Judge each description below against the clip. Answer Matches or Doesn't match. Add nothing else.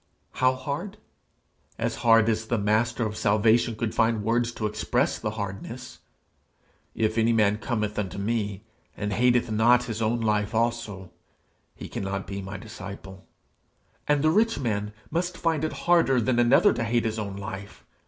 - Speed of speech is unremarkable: Matches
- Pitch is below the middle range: Matches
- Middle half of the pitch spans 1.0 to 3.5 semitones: Matches